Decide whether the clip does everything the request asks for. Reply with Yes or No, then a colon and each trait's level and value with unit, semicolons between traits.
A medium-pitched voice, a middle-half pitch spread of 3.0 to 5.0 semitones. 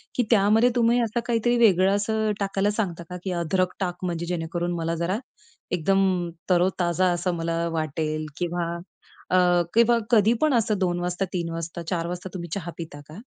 Yes: medium, 180 Hz; average, 3.3 semitones